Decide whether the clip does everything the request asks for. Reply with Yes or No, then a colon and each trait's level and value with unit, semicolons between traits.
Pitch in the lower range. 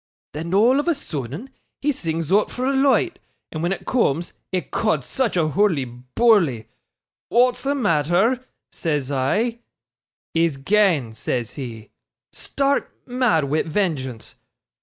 No: medium, 175 Hz